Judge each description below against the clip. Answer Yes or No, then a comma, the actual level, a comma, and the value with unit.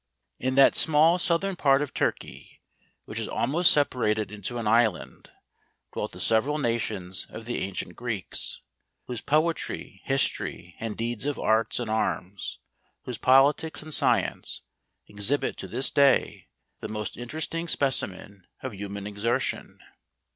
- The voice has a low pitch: Yes, low, 120 Hz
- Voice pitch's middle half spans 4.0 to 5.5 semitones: Yes, average, 5.2 semitones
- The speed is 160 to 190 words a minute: No, average, 140 wpm